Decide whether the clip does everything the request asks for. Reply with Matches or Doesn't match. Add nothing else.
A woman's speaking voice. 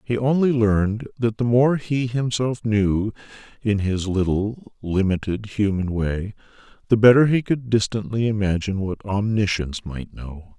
Doesn't match